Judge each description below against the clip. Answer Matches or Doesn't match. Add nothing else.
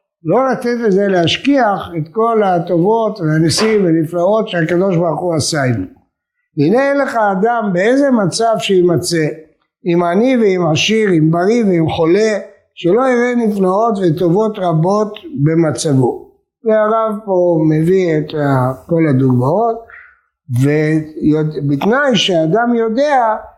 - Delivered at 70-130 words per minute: Matches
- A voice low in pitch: Doesn't match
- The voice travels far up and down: Matches